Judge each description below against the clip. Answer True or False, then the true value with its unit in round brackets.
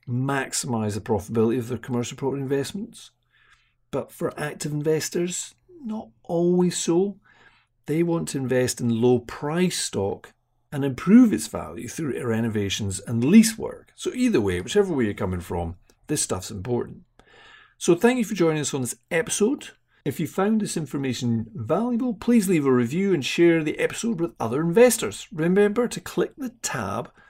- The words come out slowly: False (165 wpm)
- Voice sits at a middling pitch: True (155 Hz)